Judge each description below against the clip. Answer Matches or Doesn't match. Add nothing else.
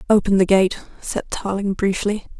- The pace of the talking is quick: Doesn't match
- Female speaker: Matches